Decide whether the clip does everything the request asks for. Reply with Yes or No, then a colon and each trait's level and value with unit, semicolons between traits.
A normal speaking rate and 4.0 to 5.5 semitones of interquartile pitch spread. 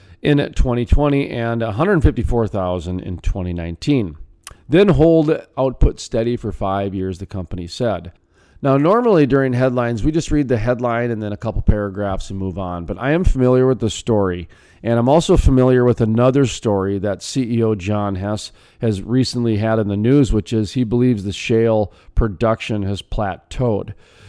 Yes: average, 165 wpm; average, 4.4 semitones